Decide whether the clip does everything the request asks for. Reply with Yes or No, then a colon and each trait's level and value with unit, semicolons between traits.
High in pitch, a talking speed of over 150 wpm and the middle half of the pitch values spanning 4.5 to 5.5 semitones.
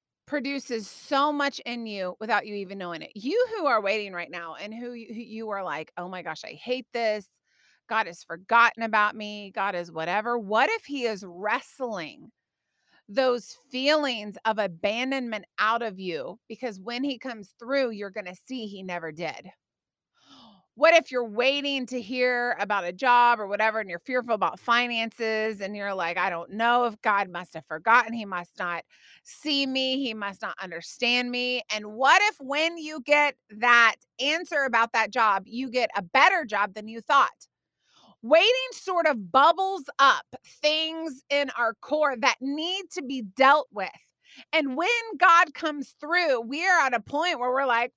Yes: high, 240 Hz; average, 180 wpm; average, 5.0 semitones